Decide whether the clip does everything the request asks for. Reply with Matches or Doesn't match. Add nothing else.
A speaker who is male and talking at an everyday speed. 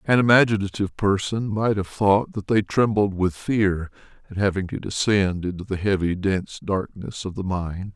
Matches